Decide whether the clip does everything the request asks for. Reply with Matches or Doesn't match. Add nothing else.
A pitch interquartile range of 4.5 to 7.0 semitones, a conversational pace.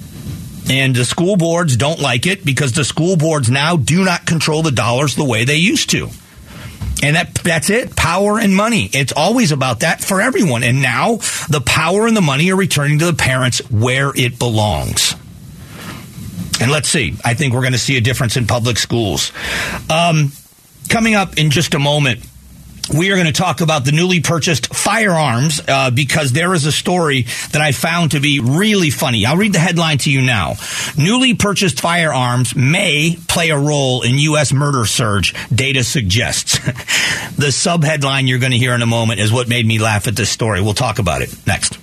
Matches